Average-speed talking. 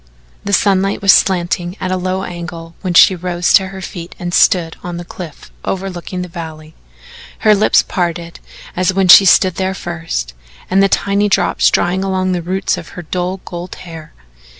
Yes: average, 180 wpm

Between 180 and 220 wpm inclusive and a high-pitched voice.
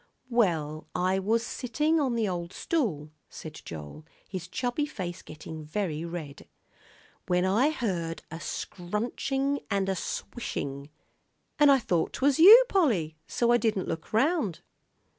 No: average, 140 wpm; high, 195 Hz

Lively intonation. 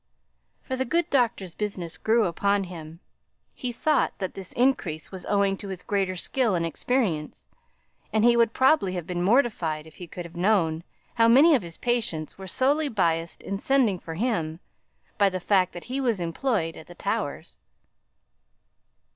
Yes: wide, 5.9 semitones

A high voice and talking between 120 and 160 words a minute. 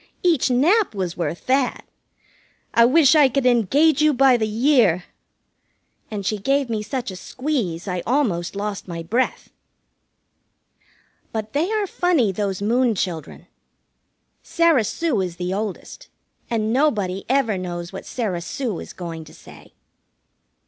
Yes: high, 225 Hz; average, 140 wpm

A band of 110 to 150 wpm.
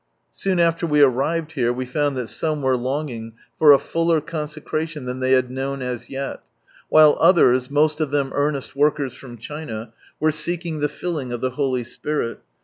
No: average, 185 wpm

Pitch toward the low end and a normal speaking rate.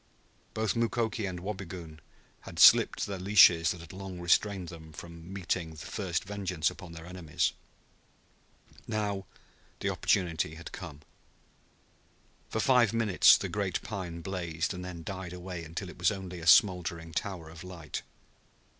Yes: very low, 90 Hz; average, 145 wpm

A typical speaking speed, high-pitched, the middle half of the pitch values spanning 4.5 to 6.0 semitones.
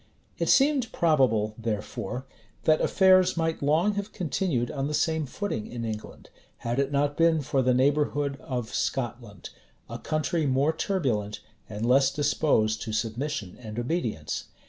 No: average, 150 wpm; medium, 140 Hz; wide, 5.4 semitones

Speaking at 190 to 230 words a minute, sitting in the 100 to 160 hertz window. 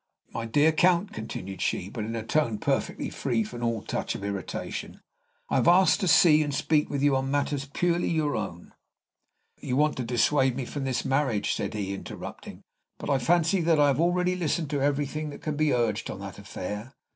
Yes: fast, 205 wpm; medium, 140 Hz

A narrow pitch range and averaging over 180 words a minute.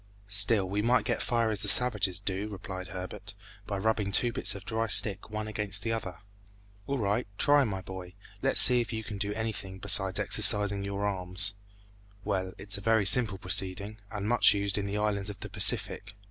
Yes: narrow, 2.2 semitones; average, 200 wpm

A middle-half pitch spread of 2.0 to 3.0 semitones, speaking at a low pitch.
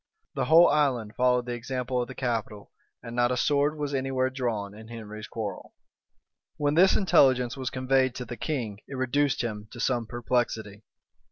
Yes: narrow, 2.6 semitones; low, 125 Hz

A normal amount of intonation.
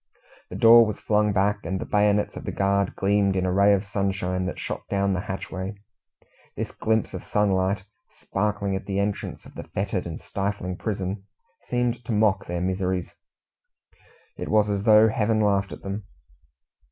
No: narrow, 1.6 semitones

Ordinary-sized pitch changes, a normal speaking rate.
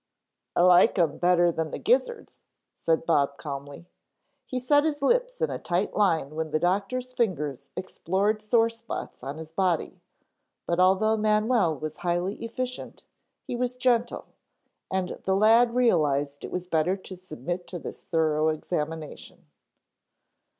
No: wide, 6.2 semitones; average, 145 wpm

